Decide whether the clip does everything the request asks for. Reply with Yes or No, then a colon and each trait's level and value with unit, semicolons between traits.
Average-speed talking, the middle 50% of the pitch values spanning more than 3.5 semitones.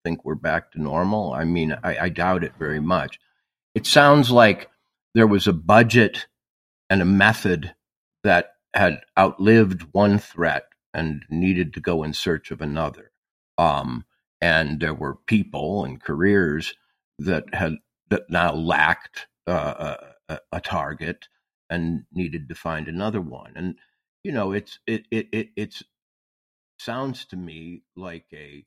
Yes: average, 150 wpm; average, 4.3 semitones